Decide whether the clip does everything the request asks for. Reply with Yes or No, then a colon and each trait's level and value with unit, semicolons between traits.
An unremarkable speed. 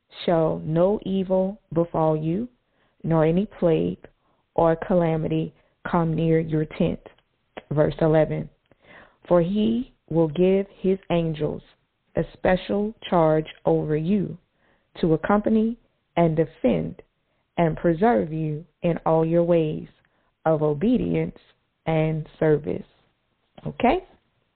No: slow, 105 wpm